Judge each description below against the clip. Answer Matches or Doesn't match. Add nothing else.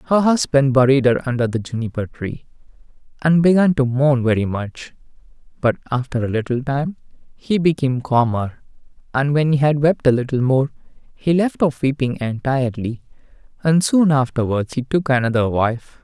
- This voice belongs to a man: Matches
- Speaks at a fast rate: Doesn't match